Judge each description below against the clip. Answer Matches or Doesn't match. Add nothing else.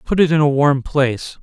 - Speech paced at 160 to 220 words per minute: Doesn't match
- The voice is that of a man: Matches